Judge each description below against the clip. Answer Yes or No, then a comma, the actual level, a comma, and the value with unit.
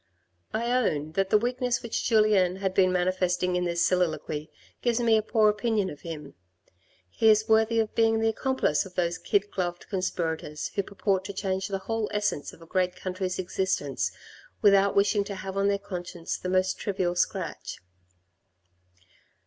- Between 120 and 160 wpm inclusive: No, average, 170 wpm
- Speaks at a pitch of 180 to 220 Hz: Yes, high, 190 Hz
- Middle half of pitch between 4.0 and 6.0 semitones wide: No, average, 3.1 semitones